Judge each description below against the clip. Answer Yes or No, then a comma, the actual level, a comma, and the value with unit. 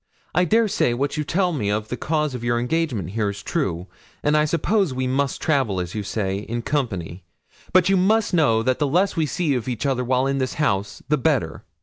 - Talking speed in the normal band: No, fast, 230 wpm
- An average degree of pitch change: No, wide, 6.0 semitones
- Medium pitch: No, low, 130 Hz